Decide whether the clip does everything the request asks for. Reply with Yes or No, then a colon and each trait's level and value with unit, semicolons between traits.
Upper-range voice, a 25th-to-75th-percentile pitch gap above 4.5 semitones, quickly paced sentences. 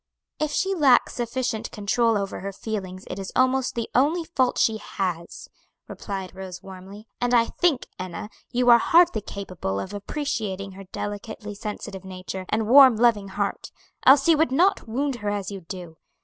No: high, 210 Hz; average, 5.0 semitones; average, 170 wpm